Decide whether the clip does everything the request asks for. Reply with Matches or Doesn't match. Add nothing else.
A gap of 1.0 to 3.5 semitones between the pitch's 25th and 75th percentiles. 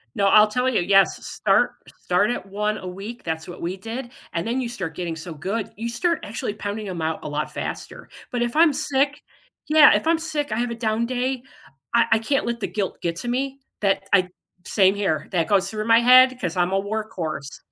Doesn't match